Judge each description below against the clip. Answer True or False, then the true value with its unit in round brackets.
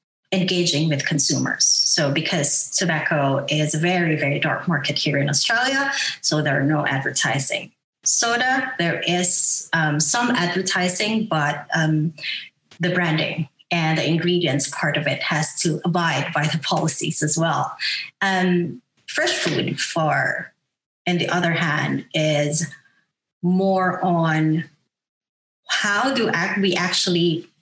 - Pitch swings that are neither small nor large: True (3.0 semitones)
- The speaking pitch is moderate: True (165 Hz)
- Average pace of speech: False (130 wpm)